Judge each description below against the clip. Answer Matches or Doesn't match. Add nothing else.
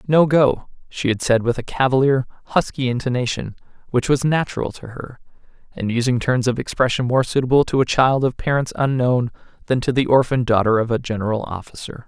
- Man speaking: Matches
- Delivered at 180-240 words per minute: Matches